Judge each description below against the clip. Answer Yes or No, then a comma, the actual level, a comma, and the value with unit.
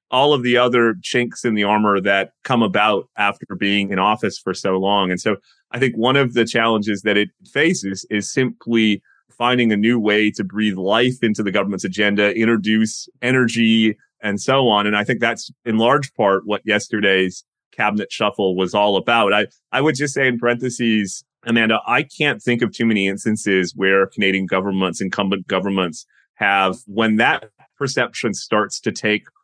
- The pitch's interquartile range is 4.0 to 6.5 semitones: No, average, 3.2 semitones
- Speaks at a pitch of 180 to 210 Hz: No, low, 105 Hz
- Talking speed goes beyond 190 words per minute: No, average, 180 wpm